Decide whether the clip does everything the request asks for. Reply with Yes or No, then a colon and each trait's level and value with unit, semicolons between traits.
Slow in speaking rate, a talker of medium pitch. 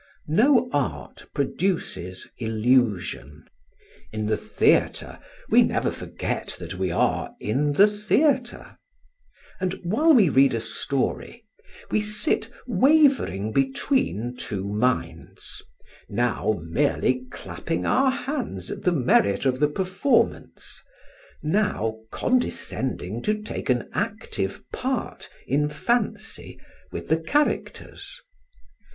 Yes: slow, 105 wpm; medium, 145 Hz